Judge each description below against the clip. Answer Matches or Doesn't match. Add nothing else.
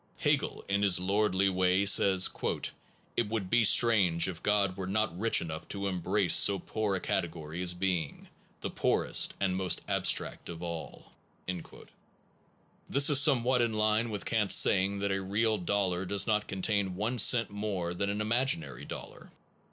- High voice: Doesn't match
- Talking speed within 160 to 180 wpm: Matches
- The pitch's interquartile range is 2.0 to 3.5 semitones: Matches